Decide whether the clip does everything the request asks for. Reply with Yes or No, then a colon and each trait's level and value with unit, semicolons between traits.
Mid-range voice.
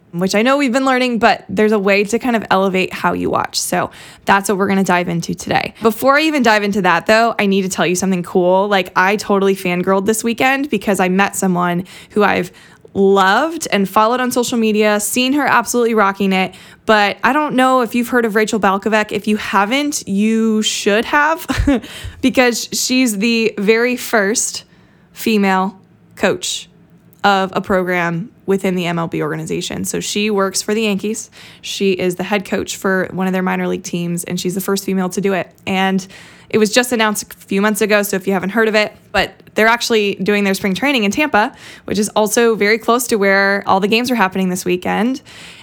No: high, 205 Hz